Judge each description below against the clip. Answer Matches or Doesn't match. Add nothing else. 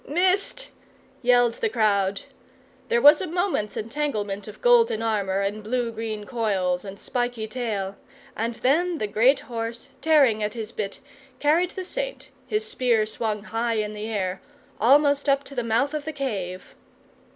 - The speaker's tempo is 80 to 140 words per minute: Doesn't match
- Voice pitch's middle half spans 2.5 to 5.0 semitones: Doesn't match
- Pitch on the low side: Doesn't match